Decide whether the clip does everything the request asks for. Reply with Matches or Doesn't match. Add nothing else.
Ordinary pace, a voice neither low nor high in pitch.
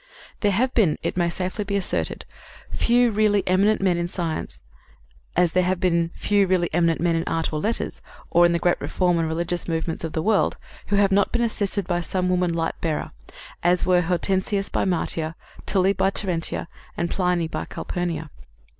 Matches